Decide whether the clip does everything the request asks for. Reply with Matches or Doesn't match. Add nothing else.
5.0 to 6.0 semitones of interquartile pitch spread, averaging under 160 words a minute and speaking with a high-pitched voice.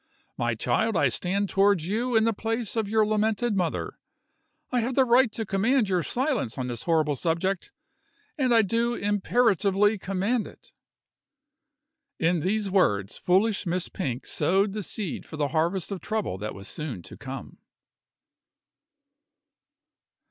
Matches